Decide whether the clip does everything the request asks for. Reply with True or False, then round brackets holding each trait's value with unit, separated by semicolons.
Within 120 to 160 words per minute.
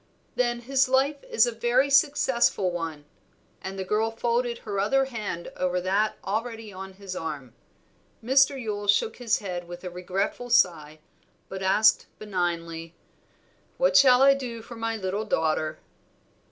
True (150 wpm)